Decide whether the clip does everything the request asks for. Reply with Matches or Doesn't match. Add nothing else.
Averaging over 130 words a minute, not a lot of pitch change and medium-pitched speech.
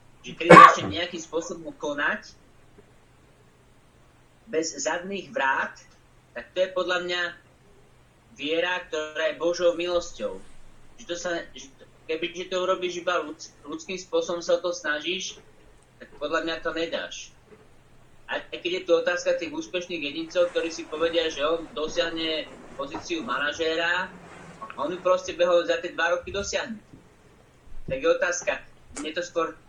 Matches